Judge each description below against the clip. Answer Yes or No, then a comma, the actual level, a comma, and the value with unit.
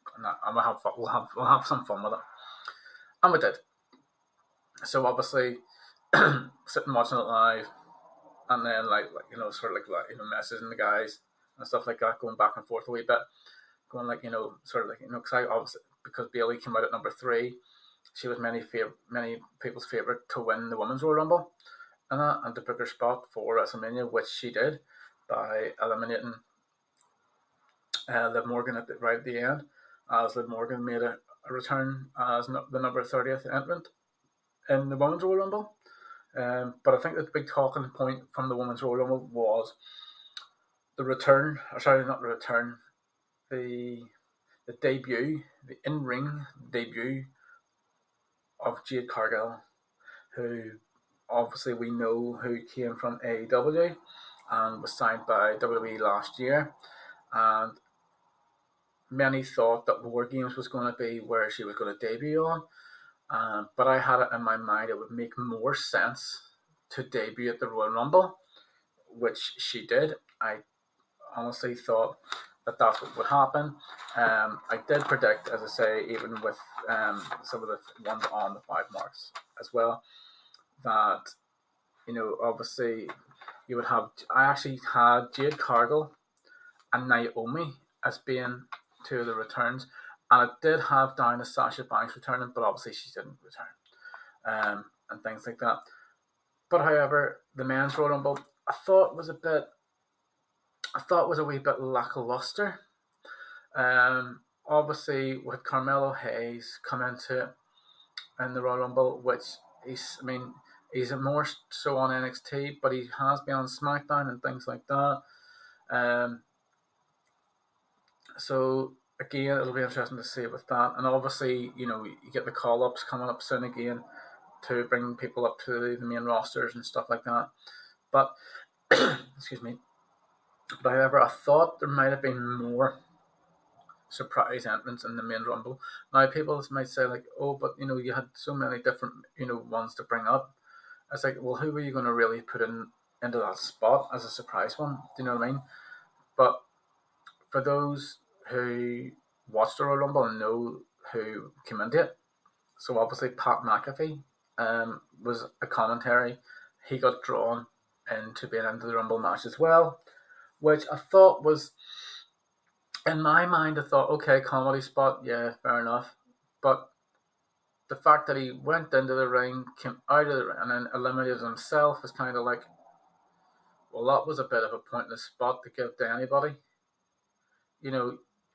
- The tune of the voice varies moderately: Yes, average, 3.3 semitones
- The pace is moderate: Yes, average, 170 wpm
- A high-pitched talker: No, low, 130 Hz